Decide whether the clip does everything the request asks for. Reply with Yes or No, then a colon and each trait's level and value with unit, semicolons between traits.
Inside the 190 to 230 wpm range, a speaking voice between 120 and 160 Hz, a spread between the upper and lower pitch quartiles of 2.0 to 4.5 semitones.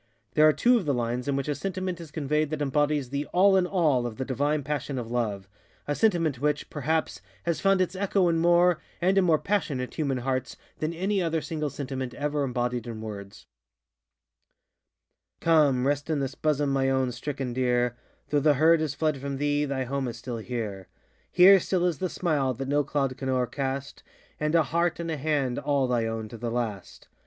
Yes: average, 200 wpm; medium, 140 Hz; average, 4.2 semitones